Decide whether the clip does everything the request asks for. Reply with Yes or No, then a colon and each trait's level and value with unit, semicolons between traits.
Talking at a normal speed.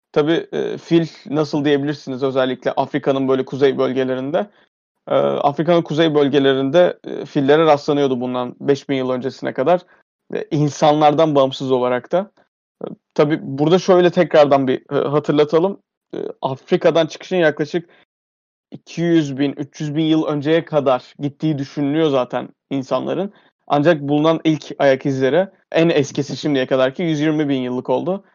Yes: average, 120 wpm